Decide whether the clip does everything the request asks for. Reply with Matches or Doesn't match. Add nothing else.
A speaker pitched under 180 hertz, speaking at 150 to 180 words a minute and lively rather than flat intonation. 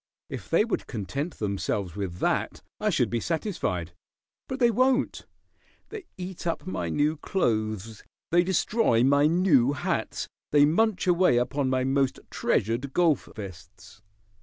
Doesn't match